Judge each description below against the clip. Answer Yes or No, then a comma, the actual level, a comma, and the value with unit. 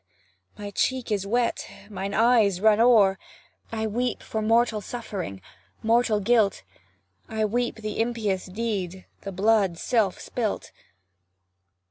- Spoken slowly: Yes, slow, 120 wpm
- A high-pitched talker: Yes, high, 215 Hz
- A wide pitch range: No, average, 2.8 semitones